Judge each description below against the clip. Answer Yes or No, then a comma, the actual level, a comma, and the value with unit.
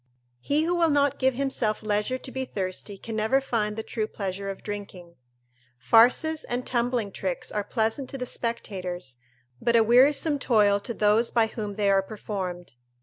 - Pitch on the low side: No, high, 220 Hz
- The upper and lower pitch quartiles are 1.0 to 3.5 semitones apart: No, average, 4.1 semitones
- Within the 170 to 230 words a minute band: Yes, average, 175 wpm